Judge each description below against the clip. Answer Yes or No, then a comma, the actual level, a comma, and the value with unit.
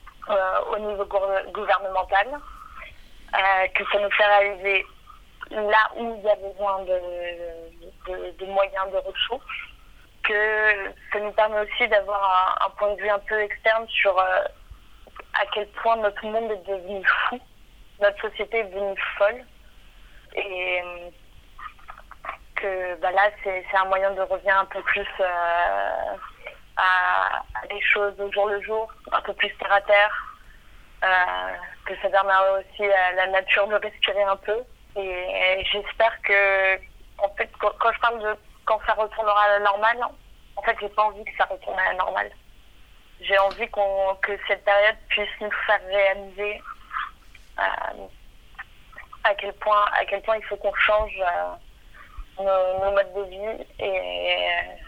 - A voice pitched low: No, high, 200 Hz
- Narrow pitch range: Yes, narrow, 1.6 semitones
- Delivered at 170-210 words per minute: No, average, 155 wpm